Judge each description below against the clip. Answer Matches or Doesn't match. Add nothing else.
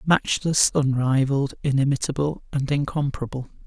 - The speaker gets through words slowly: Matches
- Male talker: Matches